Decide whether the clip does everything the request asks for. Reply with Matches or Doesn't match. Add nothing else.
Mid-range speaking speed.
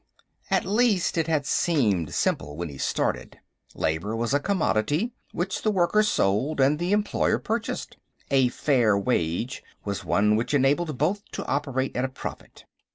Matches